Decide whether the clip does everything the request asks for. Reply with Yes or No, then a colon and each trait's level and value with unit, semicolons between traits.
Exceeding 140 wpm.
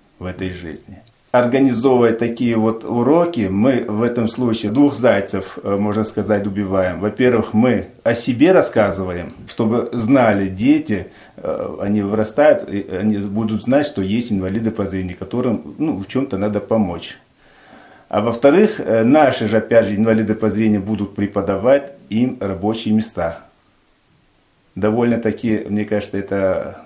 No: average, 135 wpm